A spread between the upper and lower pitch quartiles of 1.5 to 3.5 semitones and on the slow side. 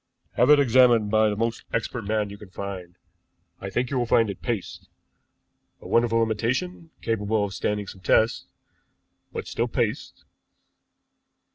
No: average, 2.7 semitones; average, 155 wpm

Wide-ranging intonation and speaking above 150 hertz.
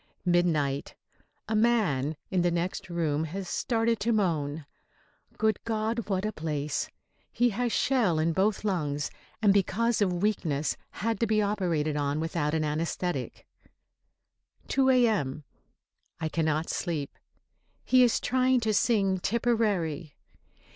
Yes: wide, 5.9 semitones; medium, 185 Hz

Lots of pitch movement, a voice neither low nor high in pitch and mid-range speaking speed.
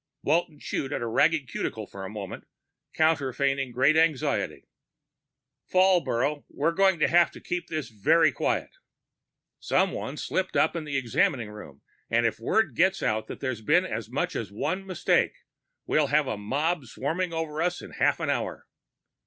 Yes: wide, 6.0 semitones; medium, 145 Hz; average, 165 wpm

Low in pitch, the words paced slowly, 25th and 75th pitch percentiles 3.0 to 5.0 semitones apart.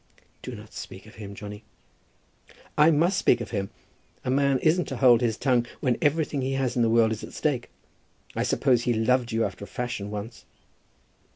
No: low, 120 Hz; average, 195 wpm; average, 3.4 semitones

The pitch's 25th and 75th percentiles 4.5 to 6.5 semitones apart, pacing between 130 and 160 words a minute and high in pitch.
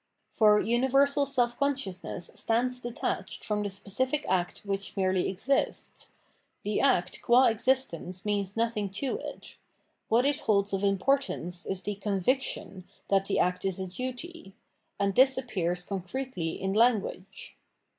Yes: average, 5.1 semitones; slow, 135 wpm; high, 210 Hz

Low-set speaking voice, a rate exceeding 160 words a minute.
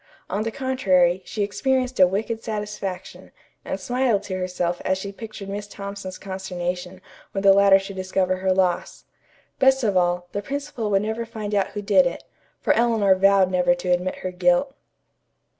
No: high, 195 Hz; average, 175 wpm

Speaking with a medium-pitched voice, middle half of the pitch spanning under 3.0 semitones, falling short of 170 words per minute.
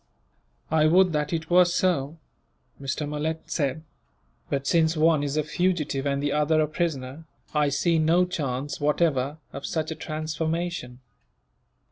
Yes: medium, 155 Hz; narrow, 2.5 semitones; average, 145 wpm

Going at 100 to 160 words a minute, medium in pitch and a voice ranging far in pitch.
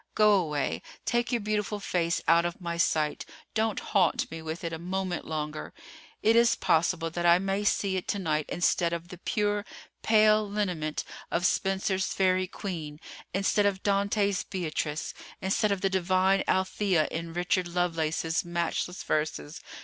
No: average, 150 wpm; medium, 180 Hz; average, 3.2 semitones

